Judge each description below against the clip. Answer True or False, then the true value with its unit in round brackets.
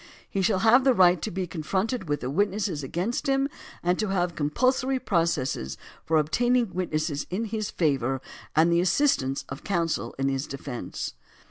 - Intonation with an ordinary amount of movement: False (6.4 semitones)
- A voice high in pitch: False (175 Hz)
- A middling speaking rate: True (170 wpm)